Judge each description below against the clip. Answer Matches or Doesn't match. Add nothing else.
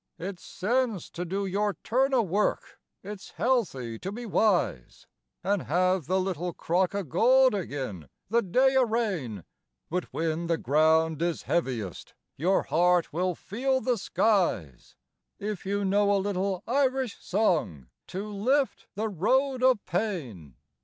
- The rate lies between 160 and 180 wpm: Doesn't match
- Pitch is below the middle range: Doesn't match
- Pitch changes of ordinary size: Matches